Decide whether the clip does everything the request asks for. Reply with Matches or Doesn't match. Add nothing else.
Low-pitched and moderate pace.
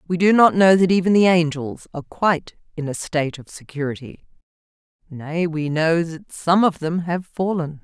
Doesn't match